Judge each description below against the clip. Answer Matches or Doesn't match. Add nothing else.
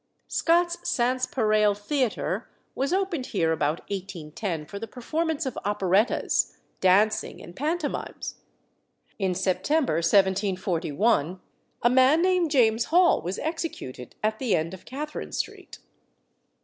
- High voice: Matches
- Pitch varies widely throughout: Matches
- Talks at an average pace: Doesn't match